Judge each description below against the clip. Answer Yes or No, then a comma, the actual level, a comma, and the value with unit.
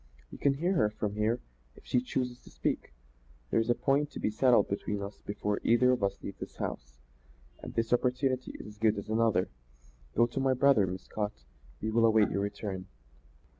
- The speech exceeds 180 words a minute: Yes, average, 200 wpm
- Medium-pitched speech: No, low, 110 Hz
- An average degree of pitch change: Yes, average, 3.6 semitones